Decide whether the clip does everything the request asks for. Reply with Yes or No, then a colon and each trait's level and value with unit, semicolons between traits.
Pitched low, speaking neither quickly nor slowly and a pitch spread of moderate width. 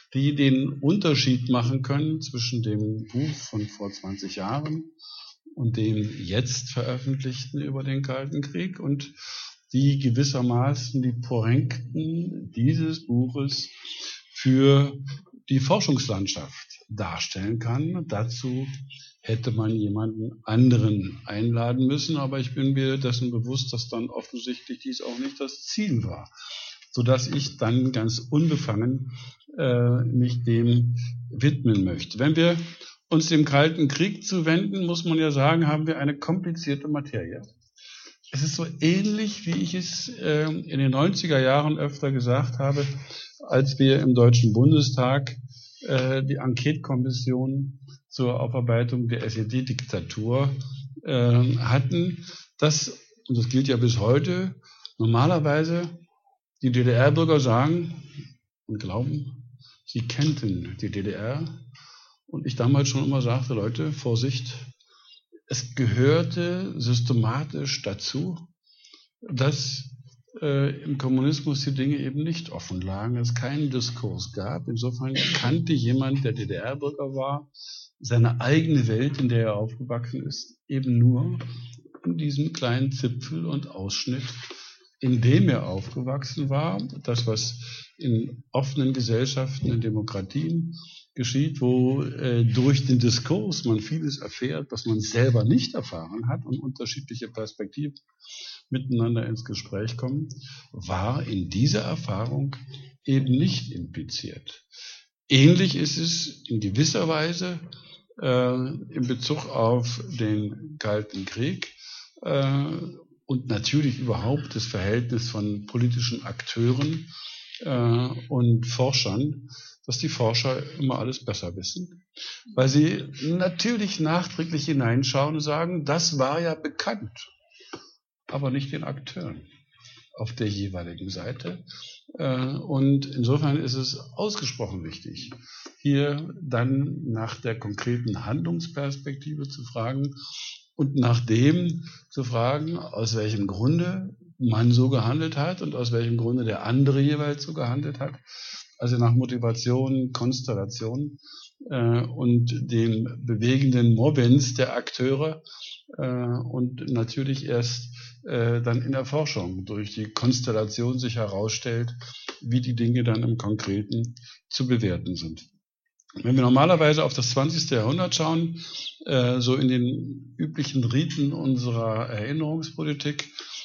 No: low, 130 Hz; slow, 120 wpm; average, 3.5 semitones